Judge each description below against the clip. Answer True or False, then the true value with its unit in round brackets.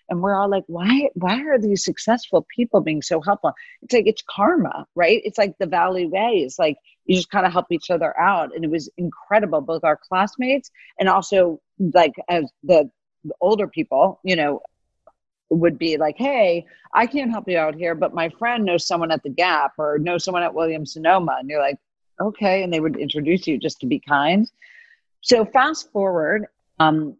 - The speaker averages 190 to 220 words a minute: True (200 wpm)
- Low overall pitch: False (185 Hz)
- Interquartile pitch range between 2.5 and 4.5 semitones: False (5.2 semitones)